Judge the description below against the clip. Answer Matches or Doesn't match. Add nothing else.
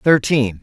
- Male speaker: Matches